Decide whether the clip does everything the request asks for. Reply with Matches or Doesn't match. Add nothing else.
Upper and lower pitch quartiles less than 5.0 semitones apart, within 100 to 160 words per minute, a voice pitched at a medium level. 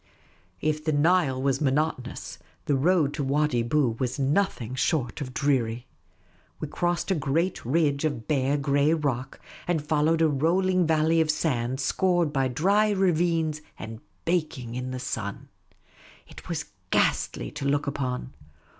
Matches